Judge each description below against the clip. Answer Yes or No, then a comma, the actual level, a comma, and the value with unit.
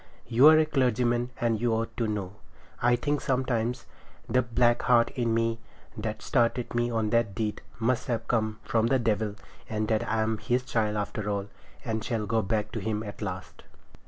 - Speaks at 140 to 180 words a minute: No, average, 190 wpm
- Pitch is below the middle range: Yes, low, 115 Hz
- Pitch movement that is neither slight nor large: No, narrow, 2.1 semitones